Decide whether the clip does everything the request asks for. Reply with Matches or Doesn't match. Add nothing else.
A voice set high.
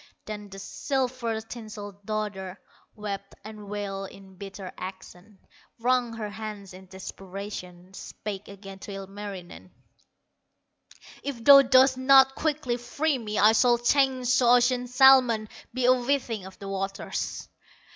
Matches